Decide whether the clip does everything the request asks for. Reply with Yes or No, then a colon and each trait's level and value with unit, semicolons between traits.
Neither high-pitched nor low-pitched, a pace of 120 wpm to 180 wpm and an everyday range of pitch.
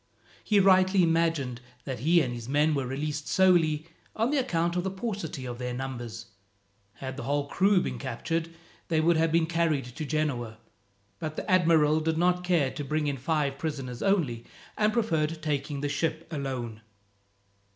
Yes: medium, 155 Hz; average, 170 wpm; average, 4.0 semitones